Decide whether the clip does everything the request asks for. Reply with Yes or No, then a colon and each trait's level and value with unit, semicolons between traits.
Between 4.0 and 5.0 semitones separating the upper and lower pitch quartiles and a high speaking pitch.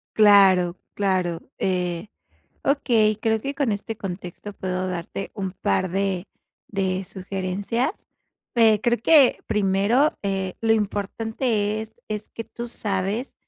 No: average, 2.9 semitones; high, 200 Hz